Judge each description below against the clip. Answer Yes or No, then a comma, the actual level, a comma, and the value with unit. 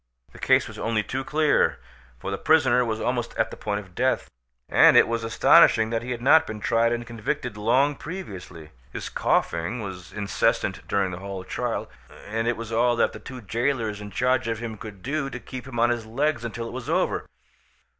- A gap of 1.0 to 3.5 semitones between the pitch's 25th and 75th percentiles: Yes, average, 3.2 semitones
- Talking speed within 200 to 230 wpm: Yes, fast, 205 wpm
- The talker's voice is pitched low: Yes, low, 115 Hz